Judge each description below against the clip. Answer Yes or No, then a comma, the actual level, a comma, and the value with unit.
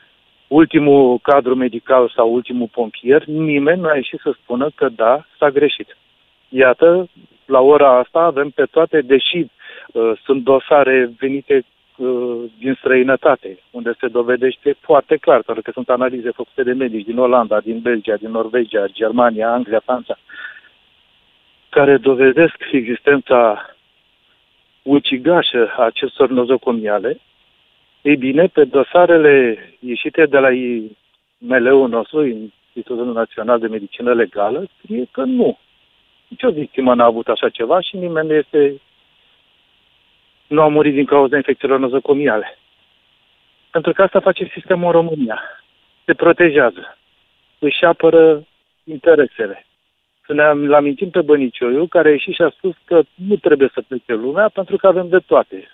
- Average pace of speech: Yes, average, 135 wpm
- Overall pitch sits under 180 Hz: Yes, medium, 140 Hz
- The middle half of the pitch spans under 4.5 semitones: No, average, 5.0 semitones